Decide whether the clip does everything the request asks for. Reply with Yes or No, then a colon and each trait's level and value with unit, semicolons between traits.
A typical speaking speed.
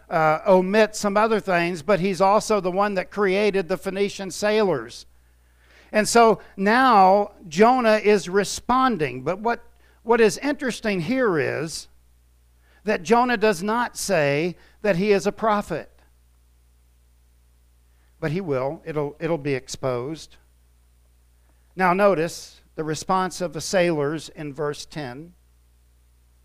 No: slow, 125 wpm